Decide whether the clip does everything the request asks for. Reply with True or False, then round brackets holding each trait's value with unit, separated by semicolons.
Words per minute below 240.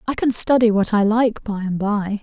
False (245 wpm)